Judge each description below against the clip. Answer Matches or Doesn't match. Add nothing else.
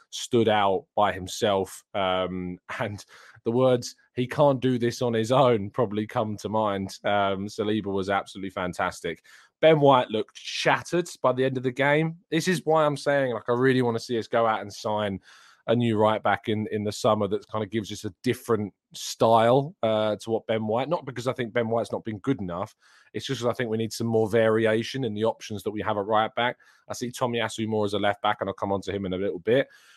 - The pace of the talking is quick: Matches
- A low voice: Matches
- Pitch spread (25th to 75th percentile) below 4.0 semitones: Matches